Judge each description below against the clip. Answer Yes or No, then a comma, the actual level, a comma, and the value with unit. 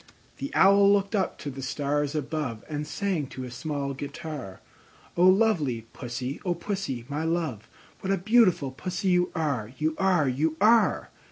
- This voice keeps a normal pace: Yes, average, 165 wpm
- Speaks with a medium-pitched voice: Yes, medium, 155 Hz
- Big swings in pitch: Yes, wide, 5.9 semitones